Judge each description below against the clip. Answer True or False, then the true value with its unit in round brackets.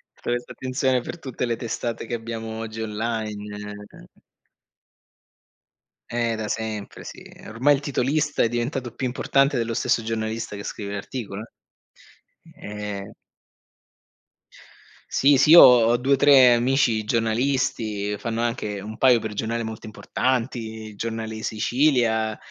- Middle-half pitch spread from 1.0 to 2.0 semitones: False (2.5 semitones)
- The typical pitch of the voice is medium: False (115 Hz)